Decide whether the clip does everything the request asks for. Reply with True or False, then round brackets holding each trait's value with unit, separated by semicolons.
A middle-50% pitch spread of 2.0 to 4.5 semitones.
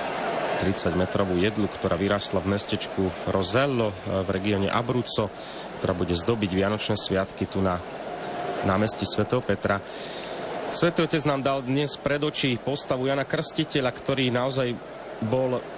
False (5.7 semitones)